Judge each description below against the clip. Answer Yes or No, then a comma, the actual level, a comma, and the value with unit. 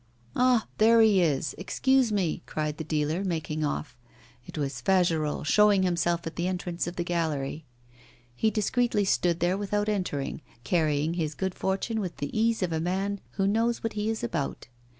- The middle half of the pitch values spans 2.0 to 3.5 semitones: No, average, 4.8 semitones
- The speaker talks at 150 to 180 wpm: Yes, average, 175 wpm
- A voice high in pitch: No, medium, 180 Hz